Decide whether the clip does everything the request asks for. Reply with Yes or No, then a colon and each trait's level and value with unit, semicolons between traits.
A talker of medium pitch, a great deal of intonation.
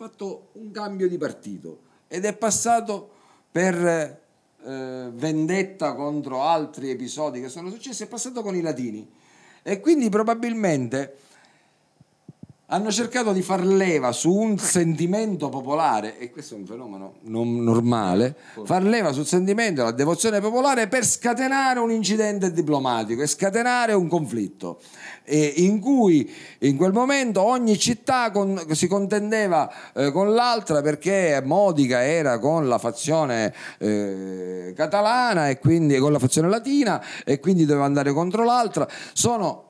Yes: medium, 175 Hz; wide, 7.4 semitones